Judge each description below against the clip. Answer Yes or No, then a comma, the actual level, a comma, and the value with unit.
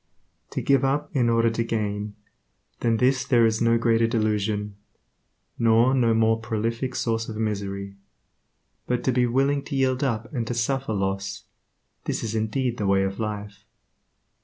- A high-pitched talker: No, low, 115 Hz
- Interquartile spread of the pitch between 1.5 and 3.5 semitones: Yes, average, 2.7 semitones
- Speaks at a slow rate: No, average, 160 wpm